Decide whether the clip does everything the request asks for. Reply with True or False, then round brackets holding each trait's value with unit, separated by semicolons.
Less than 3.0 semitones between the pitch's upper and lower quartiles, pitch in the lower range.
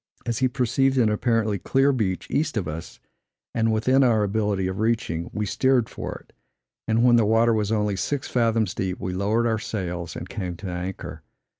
False (3.7 semitones; 110 Hz)